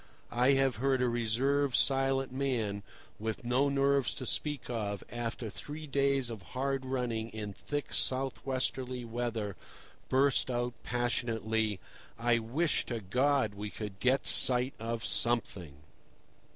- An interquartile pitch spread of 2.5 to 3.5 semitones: Yes, average, 3.1 semitones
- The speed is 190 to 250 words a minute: No, slow, 135 wpm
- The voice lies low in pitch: Yes, low, 125 Hz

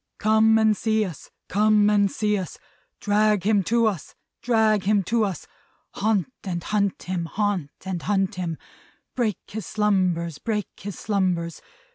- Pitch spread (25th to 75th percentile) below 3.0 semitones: Yes, narrow, 2.6 semitones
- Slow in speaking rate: No, average, 150 wpm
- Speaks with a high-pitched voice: Yes, high, 205 Hz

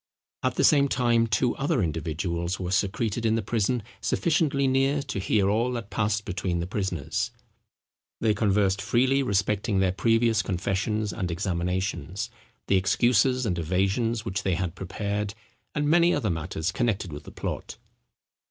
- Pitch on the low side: Yes, low, 105 Hz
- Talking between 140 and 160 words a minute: Yes, average, 150 wpm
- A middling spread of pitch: Yes, average, 4.1 semitones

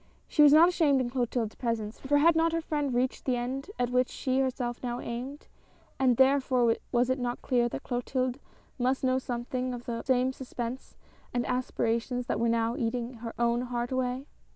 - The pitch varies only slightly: Yes, narrow, 1.7 semitones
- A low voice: No, very high, 250 Hz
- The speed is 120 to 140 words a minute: No, average, 195 wpm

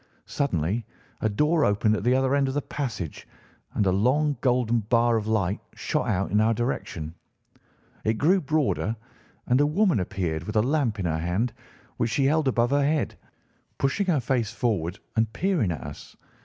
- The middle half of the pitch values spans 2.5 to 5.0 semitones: No, wide, 5.5 semitones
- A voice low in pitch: Yes, low, 120 Hz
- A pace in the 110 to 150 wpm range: No, average, 180 wpm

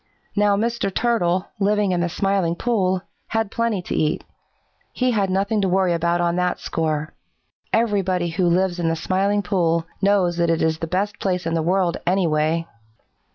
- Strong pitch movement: No, average, 2.8 semitones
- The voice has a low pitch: No, medium, 185 Hz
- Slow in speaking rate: No, average, 175 wpm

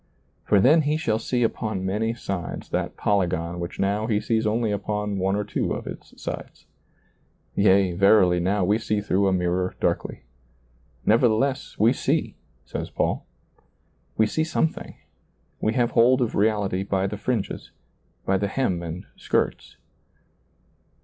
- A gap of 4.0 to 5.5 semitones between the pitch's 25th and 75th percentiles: No, average, 2.9 semitones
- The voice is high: No, low, 105 Hz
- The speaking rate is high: No, average, 150 wpm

